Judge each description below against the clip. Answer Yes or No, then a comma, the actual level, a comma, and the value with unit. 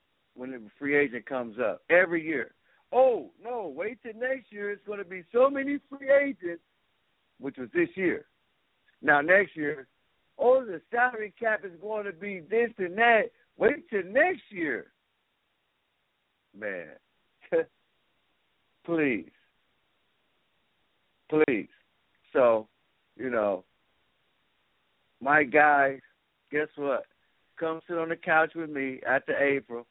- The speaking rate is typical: No, slow, 125 wpm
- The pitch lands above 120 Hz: Yes, medium, 185 Hz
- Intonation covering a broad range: Yes, wide, 8.4 semitones